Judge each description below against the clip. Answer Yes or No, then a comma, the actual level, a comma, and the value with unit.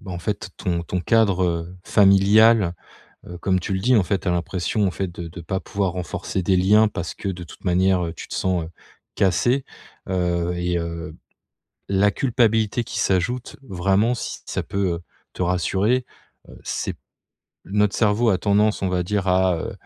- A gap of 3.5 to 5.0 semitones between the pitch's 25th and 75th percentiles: No, average, 2.8 semitones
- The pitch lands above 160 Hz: No, very low, 95 Hz